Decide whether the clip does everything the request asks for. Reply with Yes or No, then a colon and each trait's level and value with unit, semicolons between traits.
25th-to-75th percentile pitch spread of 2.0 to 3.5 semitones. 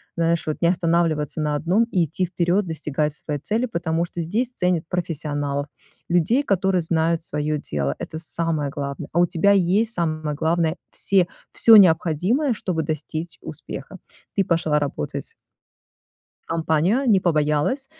Yes: average, 3.2 semitones